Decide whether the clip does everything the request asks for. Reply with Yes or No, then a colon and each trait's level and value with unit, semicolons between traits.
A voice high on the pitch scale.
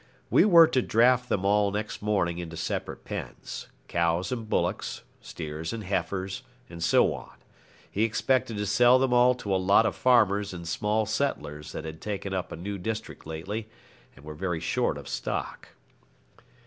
No: low, 100 Hz